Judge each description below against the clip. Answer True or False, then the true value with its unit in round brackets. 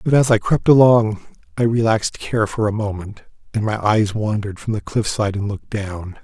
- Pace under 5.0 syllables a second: False (5.2 syllables/s)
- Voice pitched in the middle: False (105 Hz)